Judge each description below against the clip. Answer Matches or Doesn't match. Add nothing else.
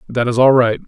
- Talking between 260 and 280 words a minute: Matches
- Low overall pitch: Matches